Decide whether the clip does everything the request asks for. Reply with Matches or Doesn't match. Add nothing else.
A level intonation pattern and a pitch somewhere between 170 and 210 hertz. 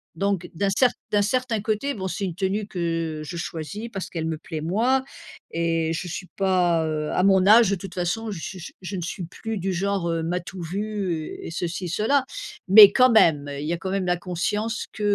Doesn't match